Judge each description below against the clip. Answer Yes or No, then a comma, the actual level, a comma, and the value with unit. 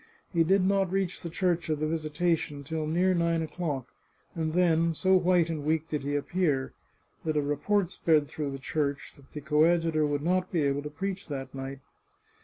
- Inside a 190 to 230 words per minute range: Yes, average, 200 wpm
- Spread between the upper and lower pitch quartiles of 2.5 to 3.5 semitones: Yes, average, 3.2 semitones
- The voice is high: No, medium, 160 Hz